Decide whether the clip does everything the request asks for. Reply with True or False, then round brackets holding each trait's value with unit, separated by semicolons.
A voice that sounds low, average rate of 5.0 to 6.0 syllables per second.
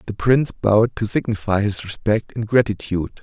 True (105 Hz; 5.5 syllables/s)